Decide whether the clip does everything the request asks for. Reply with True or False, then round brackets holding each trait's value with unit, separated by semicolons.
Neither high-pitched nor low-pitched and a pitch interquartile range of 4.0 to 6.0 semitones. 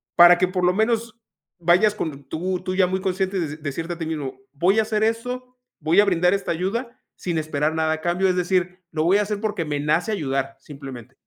True (180 Hz; 4.3 semitones)